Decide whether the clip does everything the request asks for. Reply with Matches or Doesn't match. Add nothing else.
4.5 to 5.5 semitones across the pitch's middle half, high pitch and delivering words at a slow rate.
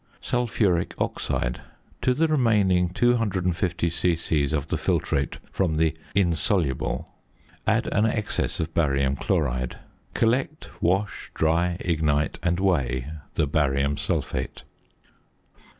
Doesn't match